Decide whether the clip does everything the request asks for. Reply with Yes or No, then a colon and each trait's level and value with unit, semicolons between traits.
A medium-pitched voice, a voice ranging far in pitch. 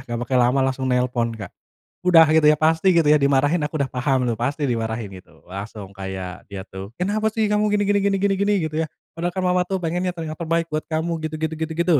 Yes: medium, 150 Hz; wide, 6.5 semitones